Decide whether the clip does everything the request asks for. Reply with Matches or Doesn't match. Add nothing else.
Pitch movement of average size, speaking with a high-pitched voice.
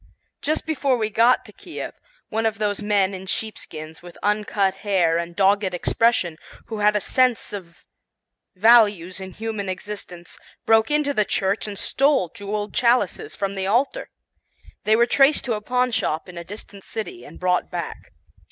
Matches